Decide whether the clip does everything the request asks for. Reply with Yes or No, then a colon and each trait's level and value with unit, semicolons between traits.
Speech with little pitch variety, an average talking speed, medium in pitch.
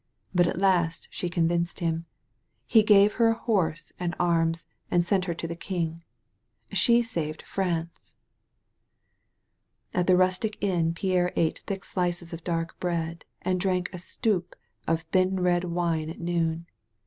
Yes: narrow, 1.8 semitones; average, 150 wpm; medium, 175 Hz